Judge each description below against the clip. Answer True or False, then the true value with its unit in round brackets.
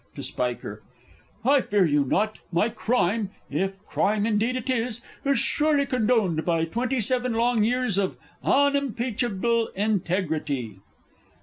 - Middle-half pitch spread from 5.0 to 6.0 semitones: True (5.3 semitones)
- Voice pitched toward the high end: True (220 Hz)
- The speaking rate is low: True (125 wpm)